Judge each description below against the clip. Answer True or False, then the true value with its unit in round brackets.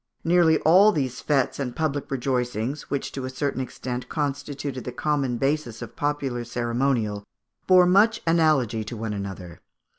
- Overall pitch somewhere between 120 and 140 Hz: True (135 Hz)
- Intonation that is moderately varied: True (3.8 semitones)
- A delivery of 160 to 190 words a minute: False (150 wpm)